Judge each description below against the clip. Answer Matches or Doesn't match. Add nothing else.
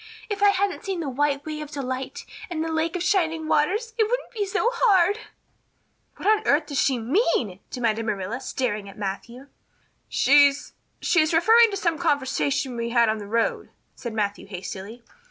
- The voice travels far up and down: Matches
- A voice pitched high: Matches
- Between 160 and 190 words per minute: Matches